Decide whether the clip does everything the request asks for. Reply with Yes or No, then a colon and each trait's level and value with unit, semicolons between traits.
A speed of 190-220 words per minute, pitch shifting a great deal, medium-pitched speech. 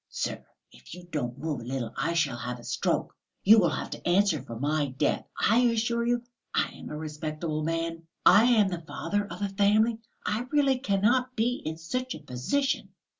Yes: average, 195 wpm; wide, 7.0 semitones; medium, 175 Hz